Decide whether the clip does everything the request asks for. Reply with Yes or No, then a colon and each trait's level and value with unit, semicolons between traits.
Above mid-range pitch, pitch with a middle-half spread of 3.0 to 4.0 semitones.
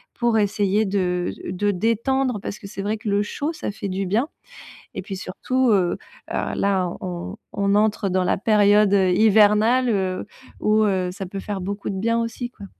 No: high, 205 Hz; narrow, 2.4 semitones